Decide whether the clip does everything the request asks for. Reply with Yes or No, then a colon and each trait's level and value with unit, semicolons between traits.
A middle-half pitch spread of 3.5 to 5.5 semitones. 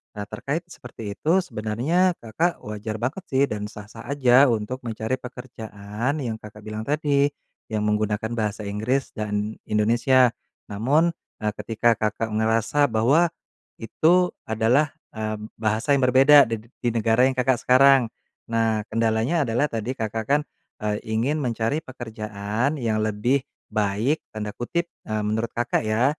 Yes: average, 3.8 semitones